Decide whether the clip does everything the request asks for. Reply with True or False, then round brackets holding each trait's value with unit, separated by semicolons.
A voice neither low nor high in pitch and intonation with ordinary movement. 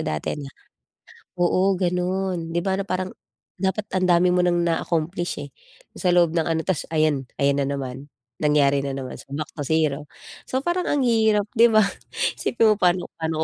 True (175 Hz; 4.2 semitones)